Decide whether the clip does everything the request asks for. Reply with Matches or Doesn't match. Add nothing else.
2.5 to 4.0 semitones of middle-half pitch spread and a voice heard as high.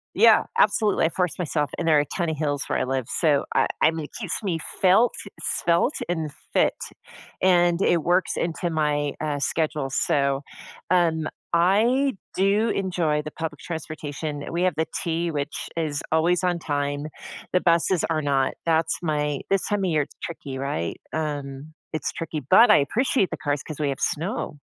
Doesn't match